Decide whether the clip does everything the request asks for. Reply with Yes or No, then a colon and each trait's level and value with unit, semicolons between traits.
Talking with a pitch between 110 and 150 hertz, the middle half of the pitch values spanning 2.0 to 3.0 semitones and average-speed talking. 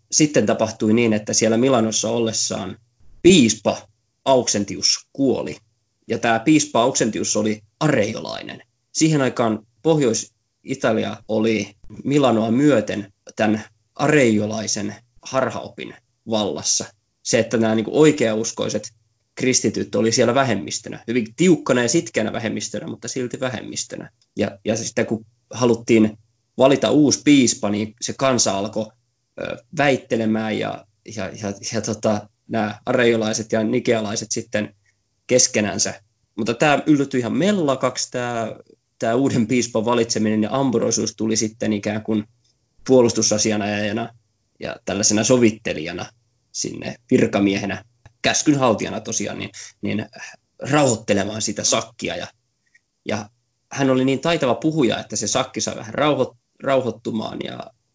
Yes: low, 115 Hz; narrow, 2.4 semitones; average, 115 wpm